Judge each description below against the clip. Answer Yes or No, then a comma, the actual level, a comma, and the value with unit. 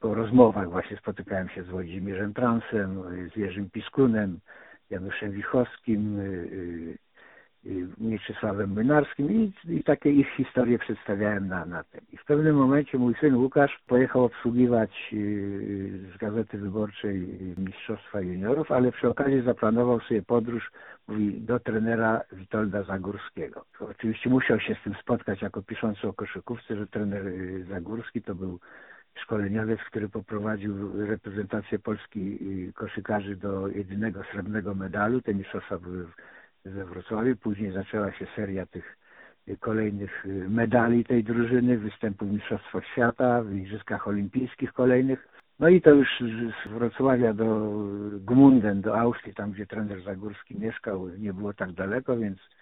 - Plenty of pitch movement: No, average, 3.1 semitones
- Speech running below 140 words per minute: Yes, average, 130 wpm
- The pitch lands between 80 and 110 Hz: Yes, low, 105 Hz